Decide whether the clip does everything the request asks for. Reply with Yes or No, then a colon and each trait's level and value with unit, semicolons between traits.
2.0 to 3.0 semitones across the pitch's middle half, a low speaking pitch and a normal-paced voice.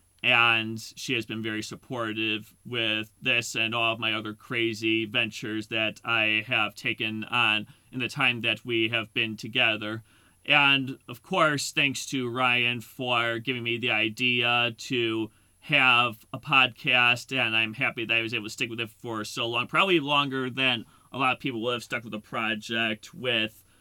Yes: narrow, 2.4 semitones; low, 115 Hz; average, 180 wpm